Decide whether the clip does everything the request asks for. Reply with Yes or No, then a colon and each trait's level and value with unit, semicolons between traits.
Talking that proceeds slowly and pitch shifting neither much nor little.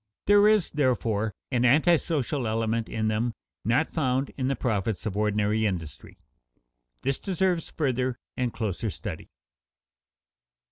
Yes: slow, 125 wpm; average, 4.7 semitones